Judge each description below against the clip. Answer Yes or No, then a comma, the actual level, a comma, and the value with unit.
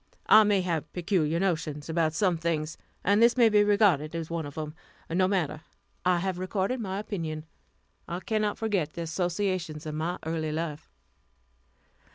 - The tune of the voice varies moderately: Yes, average, 3.8 semitones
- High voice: No, medium, 170 Hz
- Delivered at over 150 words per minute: Yes, average, 165 wpm